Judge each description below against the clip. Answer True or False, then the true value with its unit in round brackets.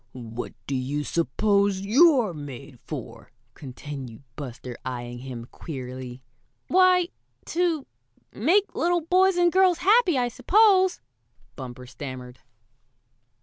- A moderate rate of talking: False (105 wpm)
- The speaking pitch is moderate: True (155 Hz)